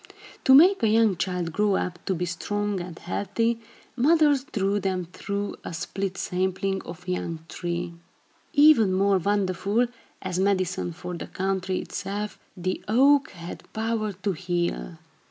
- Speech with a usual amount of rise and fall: Yes, average, 3.0 semitones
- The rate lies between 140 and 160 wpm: Yes, average, 145 wpm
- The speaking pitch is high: Yes, high, 195 Hz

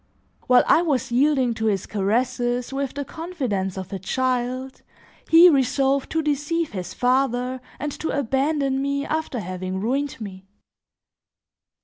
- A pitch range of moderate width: Yes, average, 3.9 semitones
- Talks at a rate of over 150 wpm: No, slow, 135 wpm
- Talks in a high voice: Yes, very high, 260 Hz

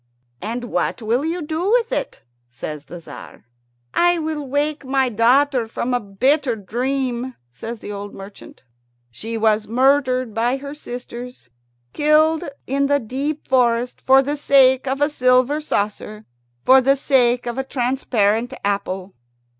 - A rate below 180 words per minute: Yes, average, 145 wpm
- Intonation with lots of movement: No, average, 3.8 semitones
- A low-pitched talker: No, very high, 255 Hz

